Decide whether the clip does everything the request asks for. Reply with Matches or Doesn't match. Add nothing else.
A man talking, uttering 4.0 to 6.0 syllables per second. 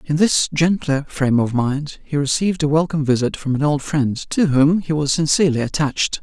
Matches